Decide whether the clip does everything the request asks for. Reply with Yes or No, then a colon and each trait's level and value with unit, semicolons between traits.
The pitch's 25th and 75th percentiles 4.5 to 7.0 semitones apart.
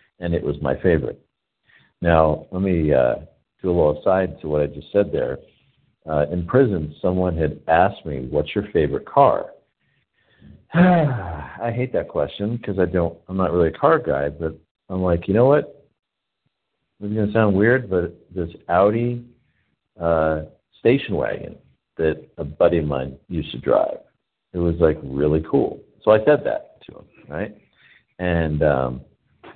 Yes: average, 5.0 semitones